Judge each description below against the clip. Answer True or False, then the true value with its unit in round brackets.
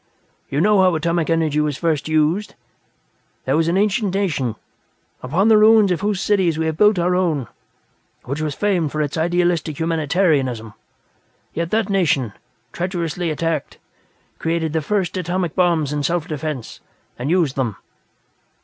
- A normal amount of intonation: True (3.4 semitones)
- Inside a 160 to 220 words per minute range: False (150 wpm)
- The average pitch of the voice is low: False (165 Hz)